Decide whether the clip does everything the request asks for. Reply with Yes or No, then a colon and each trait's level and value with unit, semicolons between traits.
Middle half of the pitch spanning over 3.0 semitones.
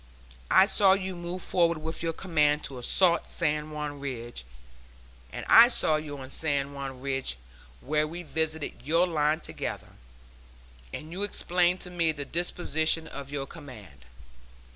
Yes: average, 3.6 semitones